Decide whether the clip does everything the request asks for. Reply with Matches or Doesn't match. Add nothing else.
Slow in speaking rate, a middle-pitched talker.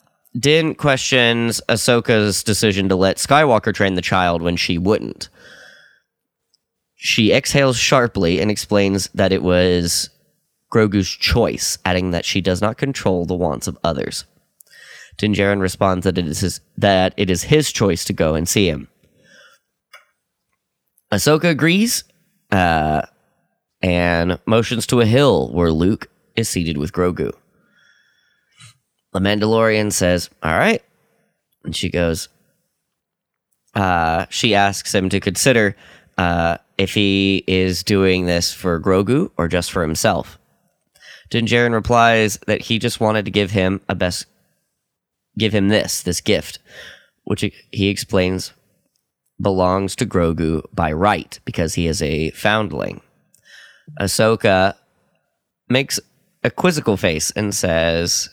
Doesn't match